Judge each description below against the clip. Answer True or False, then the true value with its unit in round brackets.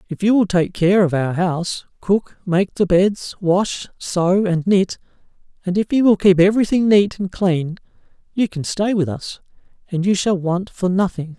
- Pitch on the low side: False (185 Hz)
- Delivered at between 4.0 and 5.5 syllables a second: True (4.5 syllables/s)